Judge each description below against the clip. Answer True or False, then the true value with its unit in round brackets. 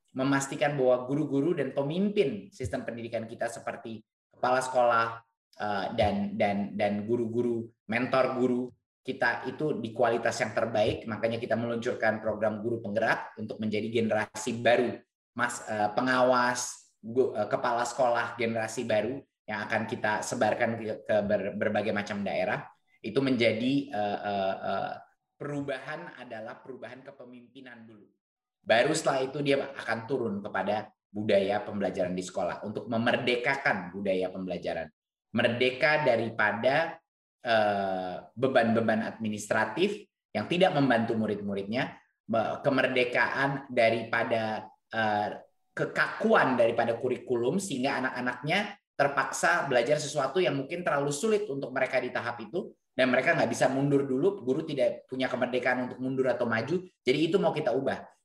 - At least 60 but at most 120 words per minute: False (130 wpm)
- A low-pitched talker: True (120 Hz)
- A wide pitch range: False (3.8 semitones)